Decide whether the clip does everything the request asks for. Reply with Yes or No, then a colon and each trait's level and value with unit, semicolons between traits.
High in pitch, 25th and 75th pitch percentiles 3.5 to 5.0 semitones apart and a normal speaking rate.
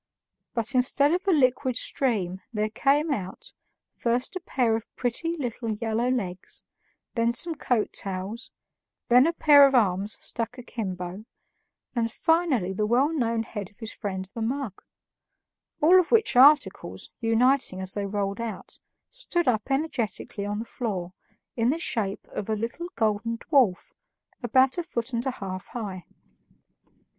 Yes: high, 235 Hz; average, 4.6 semitones; average, 150 wpm